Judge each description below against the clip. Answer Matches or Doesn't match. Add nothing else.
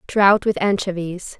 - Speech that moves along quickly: Doesn't match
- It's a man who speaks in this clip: Doesn't match